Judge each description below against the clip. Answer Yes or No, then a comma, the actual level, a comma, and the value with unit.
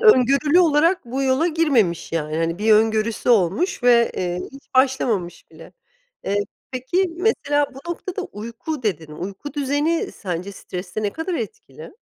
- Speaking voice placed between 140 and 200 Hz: No, very high, 250 Hz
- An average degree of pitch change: No, wide, 7.9 semitones